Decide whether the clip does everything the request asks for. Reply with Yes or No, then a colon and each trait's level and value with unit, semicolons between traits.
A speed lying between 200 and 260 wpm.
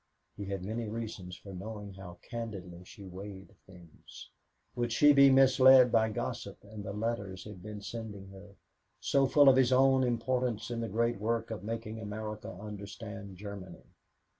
No: average, 165 wpm